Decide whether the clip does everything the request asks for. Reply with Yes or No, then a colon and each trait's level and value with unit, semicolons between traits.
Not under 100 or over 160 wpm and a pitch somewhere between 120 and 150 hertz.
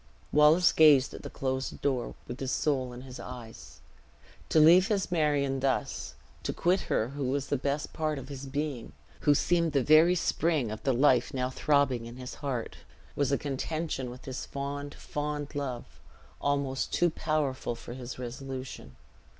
No: average, 170 wpm; medium, 140 Hz